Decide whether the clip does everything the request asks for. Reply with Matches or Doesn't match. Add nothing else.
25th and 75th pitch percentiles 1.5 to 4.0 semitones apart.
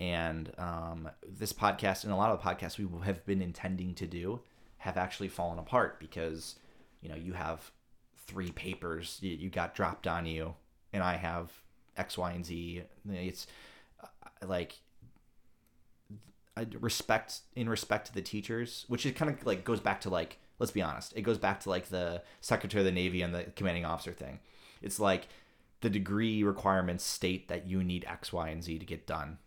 Matches